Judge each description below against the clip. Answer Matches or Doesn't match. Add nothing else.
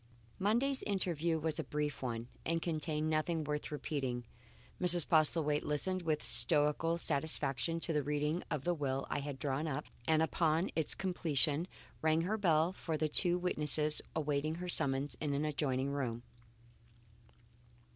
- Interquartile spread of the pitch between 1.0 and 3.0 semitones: Matches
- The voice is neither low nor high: Matches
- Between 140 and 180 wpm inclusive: Matches